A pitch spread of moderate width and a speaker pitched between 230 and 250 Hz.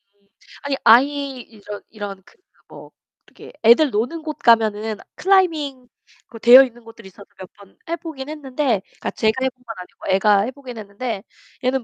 Yes: average, 4.7 semitones; high, 240 Hz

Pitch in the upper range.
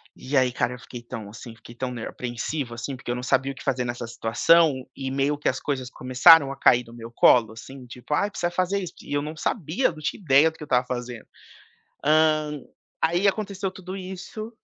No: low, 135 Hz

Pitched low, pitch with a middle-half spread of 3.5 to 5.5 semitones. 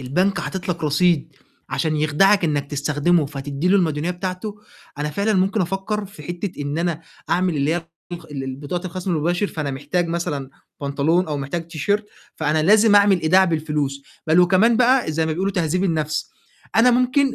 No: medium, 170 Hz; average, 4.3 semitones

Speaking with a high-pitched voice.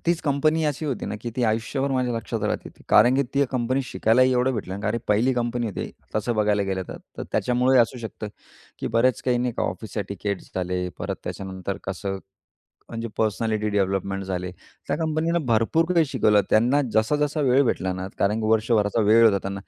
No: low, 115 Hz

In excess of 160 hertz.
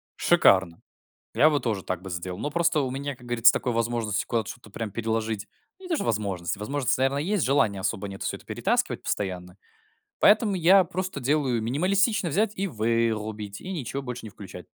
No: low, 120 Hz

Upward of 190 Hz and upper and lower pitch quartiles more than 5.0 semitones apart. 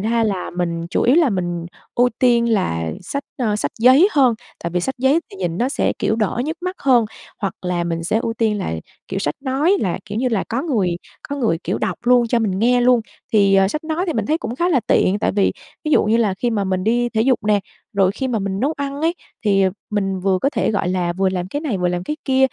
Yes: high, 220 Hz; wide, 5.4 semitones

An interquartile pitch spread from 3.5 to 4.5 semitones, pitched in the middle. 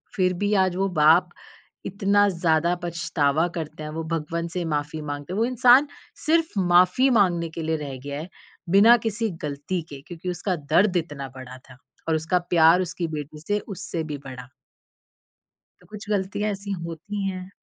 Yes: average, 4.0 semitones; medium, 175 Hz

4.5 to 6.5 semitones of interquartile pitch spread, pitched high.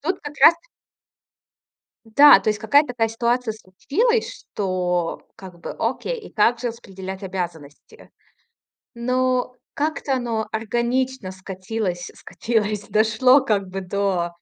Yes: average, 5.0 semitones; high, 220 Hz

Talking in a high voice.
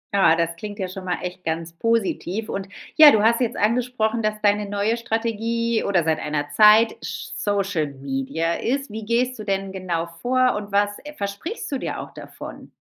Yes: high, 205 Hz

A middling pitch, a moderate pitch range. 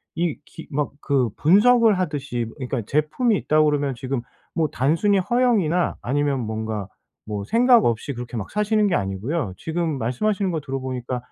No: medium, 145 Hz; wide, 6.8 semitones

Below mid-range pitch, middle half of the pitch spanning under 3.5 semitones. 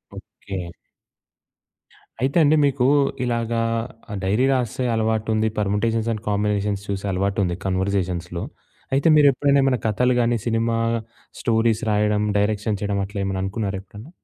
Yes: low, 105 Hz; average, 2.8 semitones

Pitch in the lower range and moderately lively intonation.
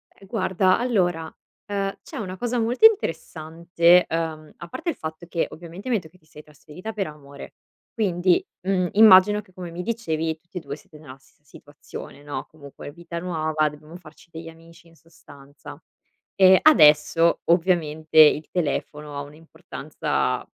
No: medium, 165 Hz; average, 3.2 semitones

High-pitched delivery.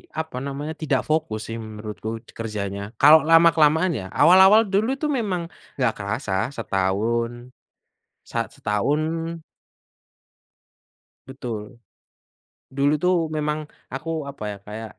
No: low, 135 Hz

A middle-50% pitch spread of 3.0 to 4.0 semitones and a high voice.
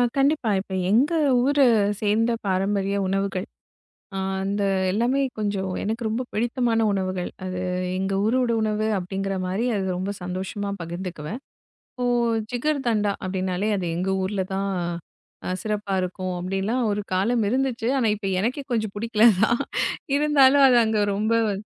Yes: average, 3.7 semitones; high, 210 Hz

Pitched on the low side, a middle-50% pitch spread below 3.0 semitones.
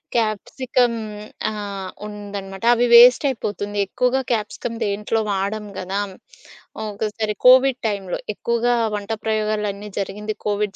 No: high, 210 Hz; narrow, 2.6 semitones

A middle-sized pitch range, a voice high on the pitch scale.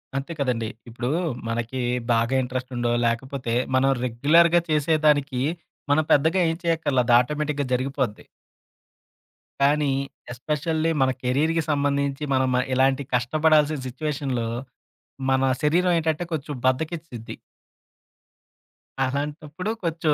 No: average, 3.4 semitones; medium, 140 Hz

